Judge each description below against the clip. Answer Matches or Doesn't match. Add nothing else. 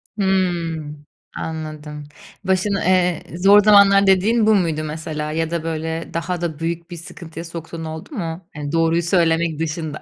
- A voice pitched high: Doesn't match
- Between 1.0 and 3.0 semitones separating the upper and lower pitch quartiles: Matches